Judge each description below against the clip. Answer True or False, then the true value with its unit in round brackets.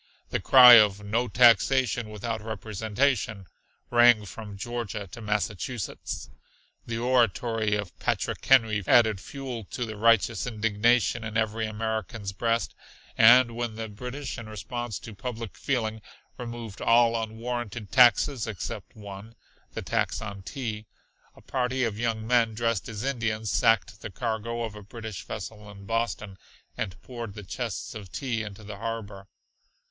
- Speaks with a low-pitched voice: True (115 Hz)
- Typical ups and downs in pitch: False (2.2 semitones)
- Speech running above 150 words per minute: False (145 wpm)